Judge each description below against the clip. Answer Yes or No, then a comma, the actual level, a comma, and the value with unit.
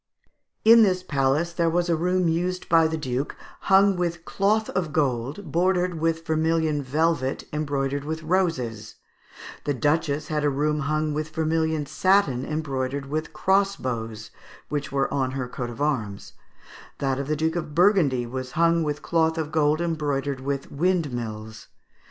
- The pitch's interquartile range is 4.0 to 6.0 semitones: No, average, 3.5 semitones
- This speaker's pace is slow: No, average, 155 wpm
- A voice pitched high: No, medium, 155 Hz